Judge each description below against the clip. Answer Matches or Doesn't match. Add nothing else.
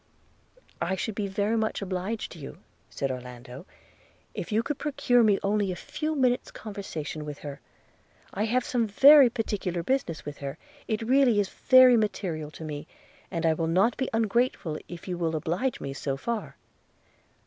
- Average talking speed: Matches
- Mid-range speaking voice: Doesn't match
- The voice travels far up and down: Matches